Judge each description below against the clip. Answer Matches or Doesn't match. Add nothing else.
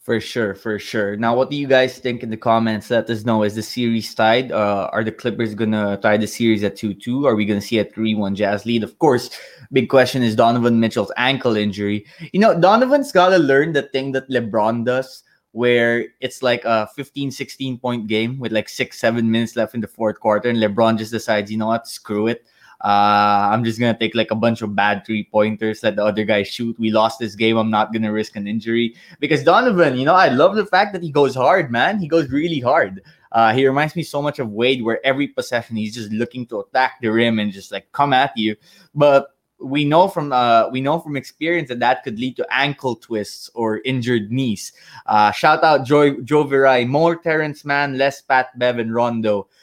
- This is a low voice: Matches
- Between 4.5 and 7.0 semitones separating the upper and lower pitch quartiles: Doesn't match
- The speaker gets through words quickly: Matches